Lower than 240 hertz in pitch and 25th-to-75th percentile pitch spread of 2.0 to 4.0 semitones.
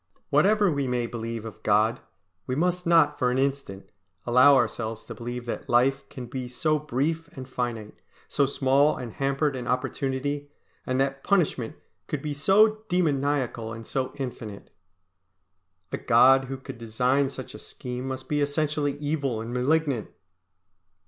Yes: low, 135 Hz; average, 3.1 semitones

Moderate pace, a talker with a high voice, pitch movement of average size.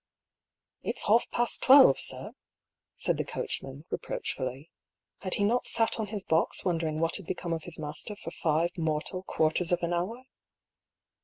No: average, 165 wpm; medium, 170 Hz; average, 4.4 semitones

